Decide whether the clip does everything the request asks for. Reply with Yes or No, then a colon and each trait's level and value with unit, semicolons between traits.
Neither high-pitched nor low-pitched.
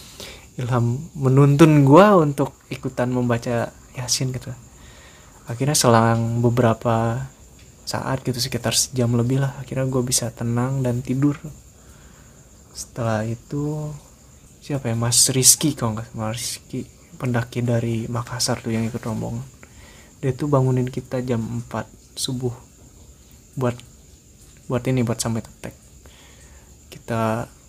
No: low, 125 Hz